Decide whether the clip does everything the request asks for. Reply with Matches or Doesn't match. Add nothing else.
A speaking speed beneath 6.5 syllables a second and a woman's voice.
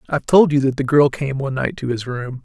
Doesn't match